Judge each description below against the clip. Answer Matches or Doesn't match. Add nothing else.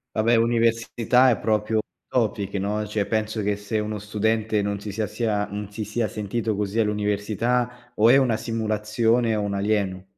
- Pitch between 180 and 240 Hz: Doesn't match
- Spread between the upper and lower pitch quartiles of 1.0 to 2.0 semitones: Matches